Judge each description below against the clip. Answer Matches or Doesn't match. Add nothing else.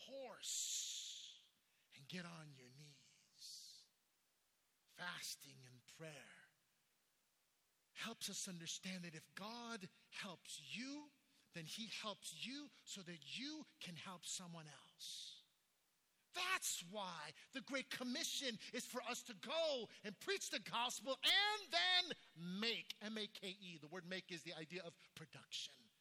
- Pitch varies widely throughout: Matches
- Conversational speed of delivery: Doesn't match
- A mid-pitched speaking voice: Doesn't match